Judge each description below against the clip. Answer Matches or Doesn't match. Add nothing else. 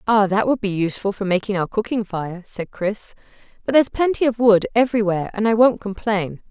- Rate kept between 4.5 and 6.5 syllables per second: Matches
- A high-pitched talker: Matches